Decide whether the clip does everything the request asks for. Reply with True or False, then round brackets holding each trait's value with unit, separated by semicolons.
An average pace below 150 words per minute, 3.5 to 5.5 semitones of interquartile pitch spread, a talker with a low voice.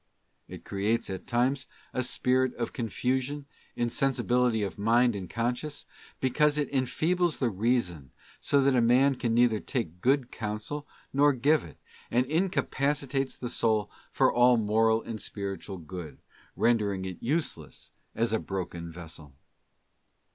True (140 wpm; 4.6 semitones; 120 Hz)